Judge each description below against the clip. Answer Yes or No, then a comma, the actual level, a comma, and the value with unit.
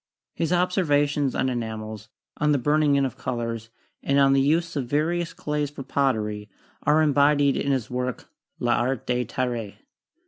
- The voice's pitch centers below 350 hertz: Yes, low, 135 Hz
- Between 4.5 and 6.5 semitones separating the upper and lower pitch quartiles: No, average, 3.5 semitones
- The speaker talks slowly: No, average, 160 wpm